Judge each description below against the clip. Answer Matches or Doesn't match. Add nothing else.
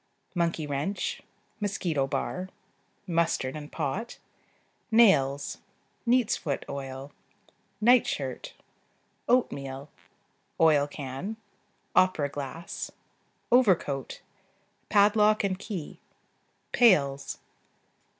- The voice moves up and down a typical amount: Doesn't match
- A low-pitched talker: Doesn't match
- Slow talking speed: Matches